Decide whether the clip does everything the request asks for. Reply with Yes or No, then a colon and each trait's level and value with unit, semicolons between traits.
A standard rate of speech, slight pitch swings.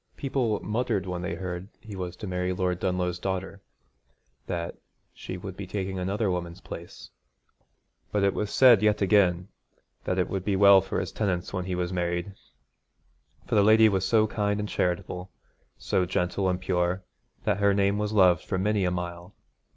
Yes: average, 180 wpm; narrow, 2.2 semitones